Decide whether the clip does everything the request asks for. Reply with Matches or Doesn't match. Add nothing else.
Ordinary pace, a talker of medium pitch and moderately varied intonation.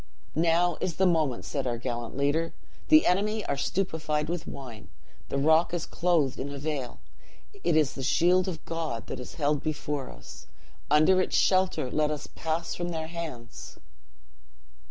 Matches